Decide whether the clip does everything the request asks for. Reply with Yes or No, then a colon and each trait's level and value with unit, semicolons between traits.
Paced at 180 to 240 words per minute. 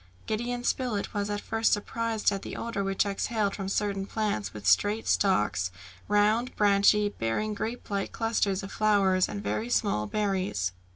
No: average, 165 wpm